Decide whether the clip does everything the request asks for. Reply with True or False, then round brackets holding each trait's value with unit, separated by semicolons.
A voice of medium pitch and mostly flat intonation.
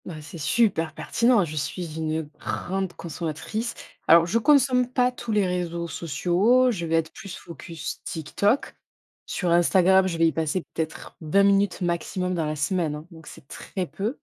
False (175 Hz; 3.8 semitones)